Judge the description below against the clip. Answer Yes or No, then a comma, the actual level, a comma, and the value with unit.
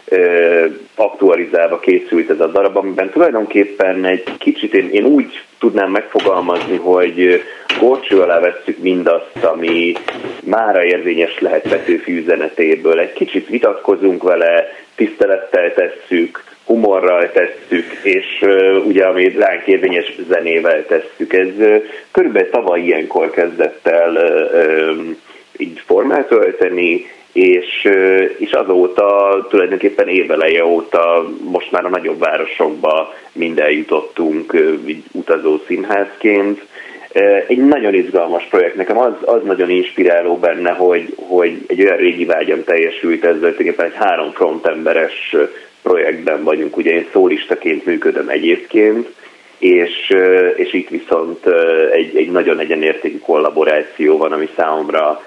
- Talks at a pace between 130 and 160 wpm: No, average, 115 wpm